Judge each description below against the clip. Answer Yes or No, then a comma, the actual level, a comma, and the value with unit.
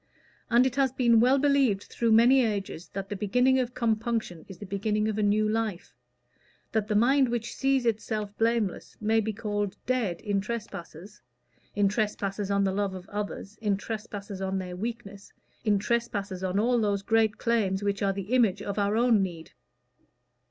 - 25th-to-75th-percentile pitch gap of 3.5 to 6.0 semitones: No, average, 2.8 semitones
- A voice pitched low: No, high, 210 Hz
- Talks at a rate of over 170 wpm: Yes, average, 180 wpm